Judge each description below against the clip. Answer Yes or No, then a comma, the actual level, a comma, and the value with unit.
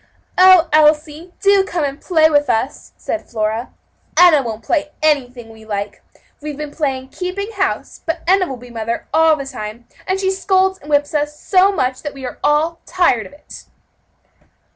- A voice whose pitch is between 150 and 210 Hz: No, very high, 300 Hz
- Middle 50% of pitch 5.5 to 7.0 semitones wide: Yes, wide, 5.9 semitones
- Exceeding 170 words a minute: Yes, average, 180 wpm